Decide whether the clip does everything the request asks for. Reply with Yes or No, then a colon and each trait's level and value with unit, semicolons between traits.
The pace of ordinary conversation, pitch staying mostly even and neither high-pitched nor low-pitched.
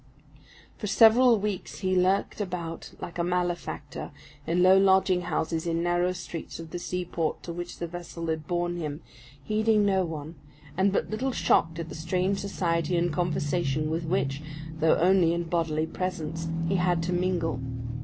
Yes: average, 165 wpm; narrow, 2.2 semitones; medium, 175 Hz